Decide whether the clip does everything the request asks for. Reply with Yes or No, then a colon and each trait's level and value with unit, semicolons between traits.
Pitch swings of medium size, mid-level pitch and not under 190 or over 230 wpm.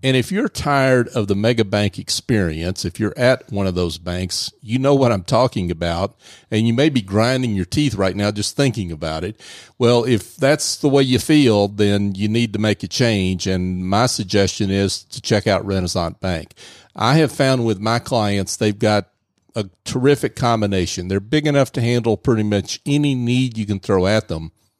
No: average, 4.2 semitones; low, 110 Hz; average, 200 wpm